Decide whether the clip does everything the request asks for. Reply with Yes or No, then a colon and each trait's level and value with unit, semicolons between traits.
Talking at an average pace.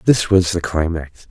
Yes: average, 185 wpm